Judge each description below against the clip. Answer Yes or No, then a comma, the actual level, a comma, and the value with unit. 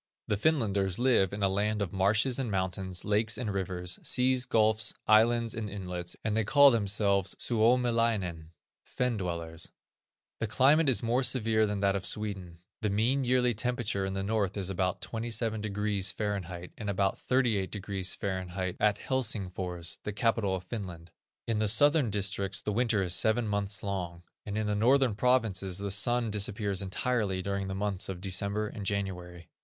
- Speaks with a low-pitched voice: Yes, low, 105 Hz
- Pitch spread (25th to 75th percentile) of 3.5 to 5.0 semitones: No, average, 3.0 semitones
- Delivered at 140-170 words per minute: Yes, average, 160 wpm